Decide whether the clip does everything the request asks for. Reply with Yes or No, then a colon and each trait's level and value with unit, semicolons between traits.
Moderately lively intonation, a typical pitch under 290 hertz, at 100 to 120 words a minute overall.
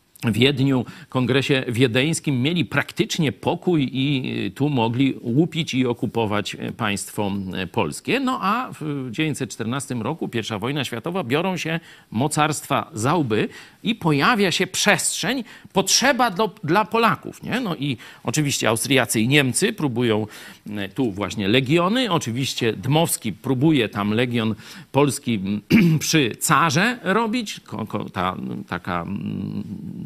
No: wide, 6.4 semitones; medium, 140 Hz; average, 115 wpm